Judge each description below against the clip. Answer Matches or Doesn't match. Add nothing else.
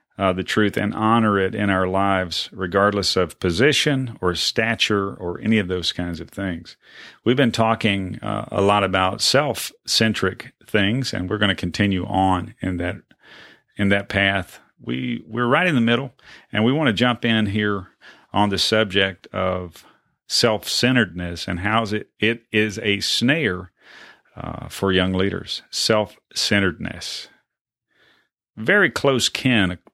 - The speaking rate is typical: Matches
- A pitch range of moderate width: Matches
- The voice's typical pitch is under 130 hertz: Matches